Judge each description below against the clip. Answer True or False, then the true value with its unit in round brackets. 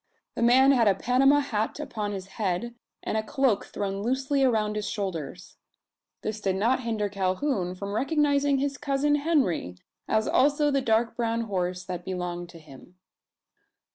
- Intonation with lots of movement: True (6.1 semitones)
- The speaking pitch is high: True (220 Hz)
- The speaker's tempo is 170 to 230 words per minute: False (160 wpm)